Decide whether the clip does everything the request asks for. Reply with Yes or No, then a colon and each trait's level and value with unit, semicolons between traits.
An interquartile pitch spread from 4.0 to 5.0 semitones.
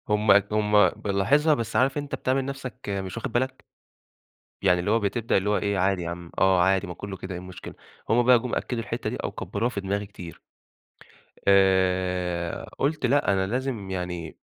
Yes: average, 4.5 semitones